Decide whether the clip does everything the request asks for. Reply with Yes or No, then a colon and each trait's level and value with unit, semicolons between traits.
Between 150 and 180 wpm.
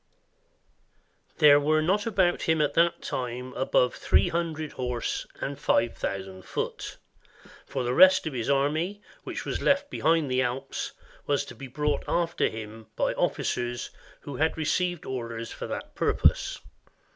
Yes: average, 155 wpm